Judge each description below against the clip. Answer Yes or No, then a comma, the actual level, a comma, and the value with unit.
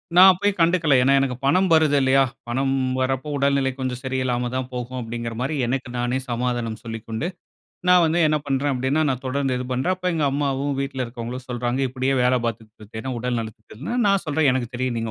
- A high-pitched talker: No, low, 130 Hz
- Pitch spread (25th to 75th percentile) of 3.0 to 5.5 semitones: No, narrow, 2.5 semitones